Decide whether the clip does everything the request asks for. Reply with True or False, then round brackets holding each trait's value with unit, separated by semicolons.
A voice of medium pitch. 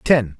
False (120 Hz)